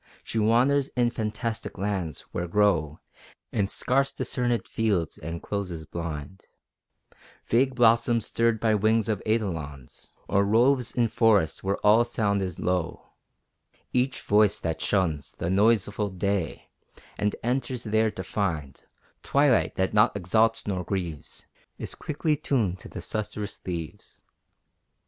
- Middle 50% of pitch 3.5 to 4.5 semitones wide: Yes, average, 4.2 semitones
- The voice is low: Yes, low, 105 Hz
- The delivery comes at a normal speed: No, slow, 130 wpm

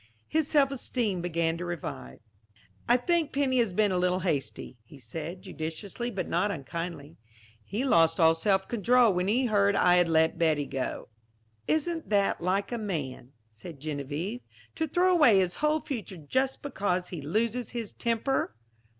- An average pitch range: No, wide, 6.9 semitones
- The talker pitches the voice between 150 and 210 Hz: Yes, high, 190 Hz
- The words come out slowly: No, average, 165 wpm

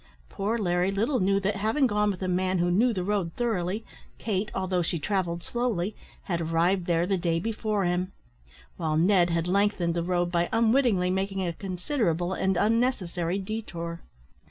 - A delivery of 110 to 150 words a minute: No, average, 170 wpm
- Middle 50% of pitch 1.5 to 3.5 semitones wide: Yes, average, 3.2 semitones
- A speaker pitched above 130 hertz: Yes, medium, 185 Hz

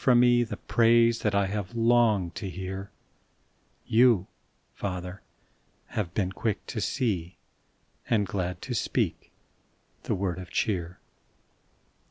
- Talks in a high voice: No, low, 100 Hz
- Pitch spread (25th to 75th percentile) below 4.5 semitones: Yes, average, 4.0 semitones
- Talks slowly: Yes, slow, 125 wpm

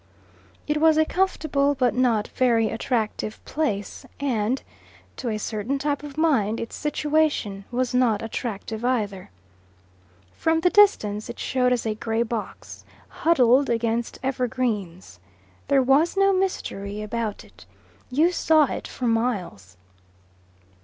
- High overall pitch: Yes, high, 245 Hz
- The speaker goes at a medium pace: No, slow, 130 wpm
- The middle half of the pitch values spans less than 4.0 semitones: No, average, 5.0 semitones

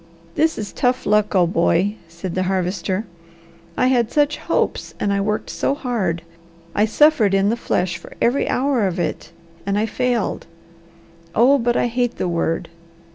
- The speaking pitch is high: Yes, high, 210 Hz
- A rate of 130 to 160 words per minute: No, average, 170 wpm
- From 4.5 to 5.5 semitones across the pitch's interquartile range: Yes, average, 4.9 semitones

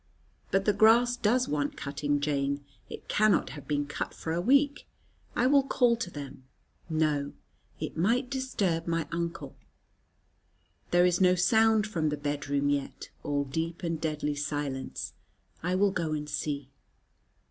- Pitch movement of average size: No, wide, 6.3 semitones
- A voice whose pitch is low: No, medium, 165 Hz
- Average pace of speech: Yes, average, 155 wpm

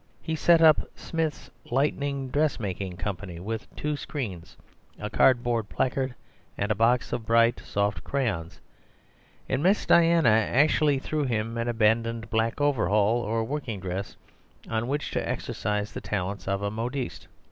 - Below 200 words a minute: Yes, average, 140 wpm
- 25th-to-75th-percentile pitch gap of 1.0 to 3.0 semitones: No, average, 5.2 semitones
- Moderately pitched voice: No, low, 115 Hz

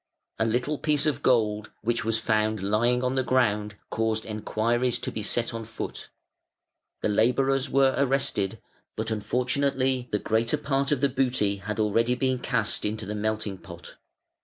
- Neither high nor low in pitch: No, low, 115 Hz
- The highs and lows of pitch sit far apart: No, average, 3.3 semitones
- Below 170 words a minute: Yes, average, 160 wpm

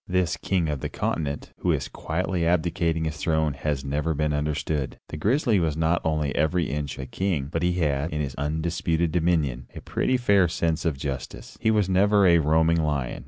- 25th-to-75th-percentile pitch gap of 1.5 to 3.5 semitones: Yes, average, 3.0 semitones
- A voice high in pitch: No, very low, 80 Hz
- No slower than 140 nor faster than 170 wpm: No, average, 195 wpm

